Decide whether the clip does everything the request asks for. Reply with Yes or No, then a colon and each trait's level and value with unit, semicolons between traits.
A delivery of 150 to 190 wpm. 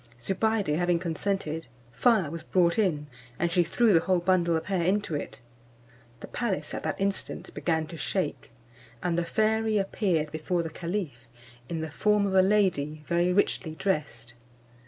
Yes: average, 165 wpm